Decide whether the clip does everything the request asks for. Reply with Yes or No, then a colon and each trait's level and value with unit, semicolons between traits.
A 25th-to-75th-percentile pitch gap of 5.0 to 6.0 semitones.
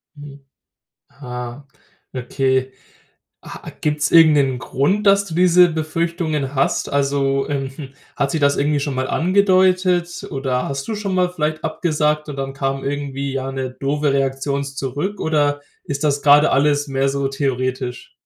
No: narrow, 2.6 semitones